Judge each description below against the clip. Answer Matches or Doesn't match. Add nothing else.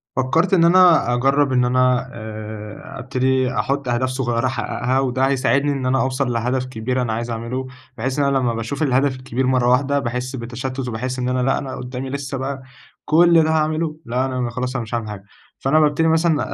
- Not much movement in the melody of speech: Matches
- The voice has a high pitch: Doesn't match